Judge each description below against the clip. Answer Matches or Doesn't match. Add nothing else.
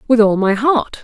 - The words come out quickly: Matches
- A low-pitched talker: Doesn't match